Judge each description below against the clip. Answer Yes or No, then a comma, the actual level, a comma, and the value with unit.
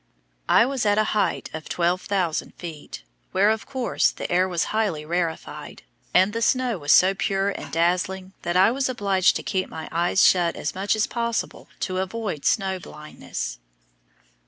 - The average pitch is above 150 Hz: Yes, high, 190 Hz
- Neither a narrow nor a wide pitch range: Yes, average, 3.7 semitones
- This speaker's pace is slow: No, average, 170 wpm